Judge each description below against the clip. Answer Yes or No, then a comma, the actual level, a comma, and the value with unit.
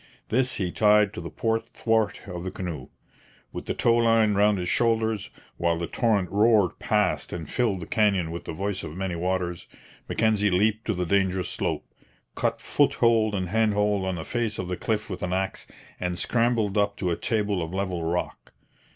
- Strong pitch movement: No, average, 3.5 semitones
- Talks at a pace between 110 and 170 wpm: No, average, 190 wpm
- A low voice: Yes, low, 100 Hz